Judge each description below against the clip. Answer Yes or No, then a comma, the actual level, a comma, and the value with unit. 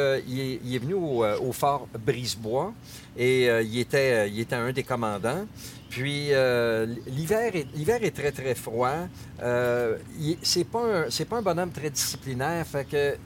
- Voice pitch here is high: No, low, 130 Hz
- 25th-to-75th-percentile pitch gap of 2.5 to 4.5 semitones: Yes, average, 3.1 semitones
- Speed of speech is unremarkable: Yes, average, 185 wpm